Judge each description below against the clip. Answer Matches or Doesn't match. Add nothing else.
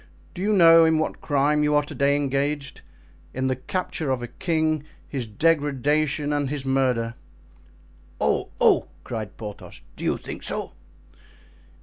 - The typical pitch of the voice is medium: Matches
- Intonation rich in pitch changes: Doesn't match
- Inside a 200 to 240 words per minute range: Doesn't match